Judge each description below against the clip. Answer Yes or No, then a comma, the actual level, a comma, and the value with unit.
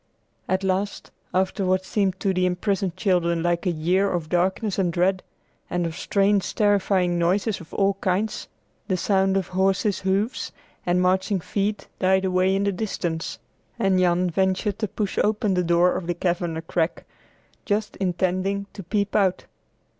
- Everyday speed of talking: Yes, average, 165 wpm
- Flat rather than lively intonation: Yes, narrow, 1.9 semitones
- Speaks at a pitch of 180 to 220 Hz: Yes, high, 190 Hz